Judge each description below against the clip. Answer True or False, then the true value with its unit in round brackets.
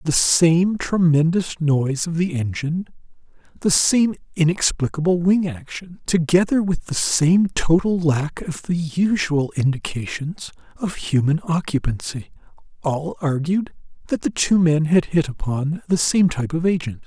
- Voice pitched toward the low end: False (160 Hz)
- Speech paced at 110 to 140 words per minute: True (135 wpm)